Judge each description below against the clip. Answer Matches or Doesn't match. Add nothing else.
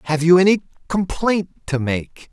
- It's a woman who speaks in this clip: Doesn't match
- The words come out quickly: Doesn't match